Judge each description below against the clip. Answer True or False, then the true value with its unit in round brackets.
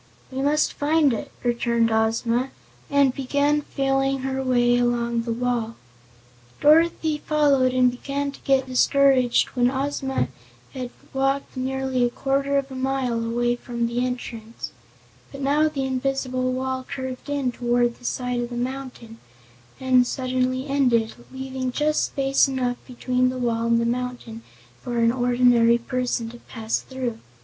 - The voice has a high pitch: True (255 Hz)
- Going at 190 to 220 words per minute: False (150 wpm)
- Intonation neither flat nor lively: False (2.0 semitones)